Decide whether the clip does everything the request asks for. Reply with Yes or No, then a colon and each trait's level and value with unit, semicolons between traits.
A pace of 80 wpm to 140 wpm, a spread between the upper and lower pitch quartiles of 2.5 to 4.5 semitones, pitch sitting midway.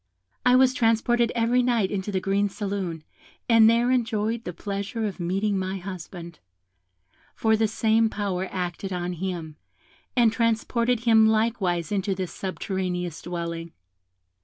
No: slow, 135 wpm; average, 3.8 semitones; high, 200 Hz